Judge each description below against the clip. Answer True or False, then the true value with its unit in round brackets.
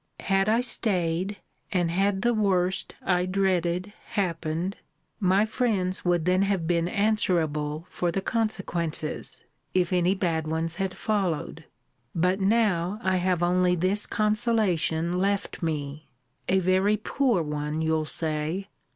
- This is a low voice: False (185 Hz)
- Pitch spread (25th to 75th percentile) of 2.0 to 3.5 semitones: True (3.0 semitones)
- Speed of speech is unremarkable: False (130 wpm)